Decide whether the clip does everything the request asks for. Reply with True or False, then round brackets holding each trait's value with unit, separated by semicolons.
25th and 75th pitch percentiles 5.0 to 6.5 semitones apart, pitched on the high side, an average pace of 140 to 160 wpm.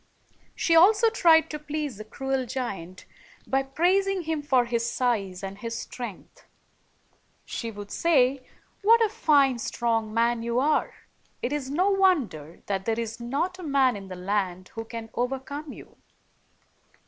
True (5.5 semitones; 255 Hz; 155 wpm)